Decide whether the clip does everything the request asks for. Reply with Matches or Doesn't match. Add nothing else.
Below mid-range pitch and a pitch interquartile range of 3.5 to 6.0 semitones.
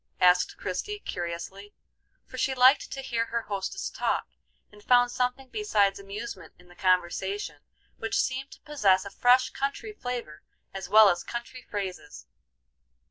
Doesn't match